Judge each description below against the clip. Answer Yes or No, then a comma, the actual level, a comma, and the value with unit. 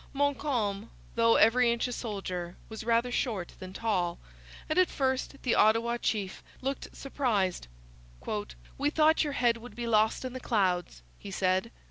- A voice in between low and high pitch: No, high, 230 Hz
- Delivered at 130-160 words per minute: Yes, average, 155 wpm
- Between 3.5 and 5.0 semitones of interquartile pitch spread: Yes, average, 4.4 semitones